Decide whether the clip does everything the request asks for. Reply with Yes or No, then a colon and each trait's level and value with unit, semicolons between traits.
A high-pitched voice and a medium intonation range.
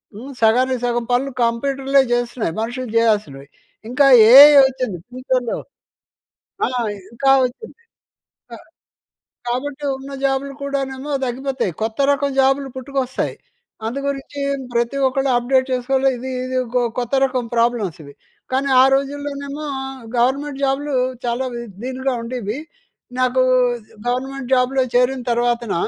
No: very high, 255 Hz; narrow, 2.2 semitones